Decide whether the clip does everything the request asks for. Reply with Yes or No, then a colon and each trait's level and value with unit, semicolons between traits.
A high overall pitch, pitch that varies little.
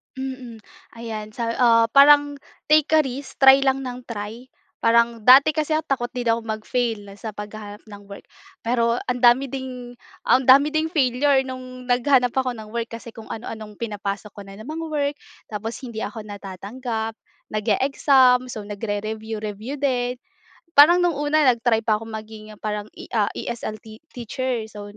No: high, 235 Hz; average, 3.4 semitones